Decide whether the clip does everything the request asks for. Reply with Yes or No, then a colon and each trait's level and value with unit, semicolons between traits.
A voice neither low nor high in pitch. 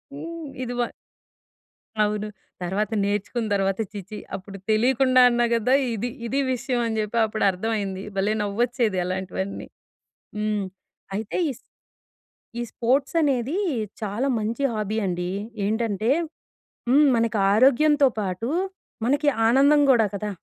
No: high, 220 Hz